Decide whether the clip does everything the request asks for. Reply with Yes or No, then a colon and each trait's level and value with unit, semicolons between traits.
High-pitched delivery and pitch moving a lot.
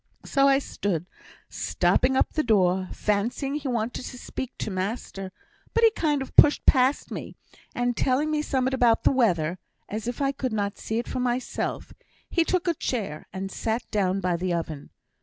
Yes: high, 240 Hz; wide, 5.7 semitones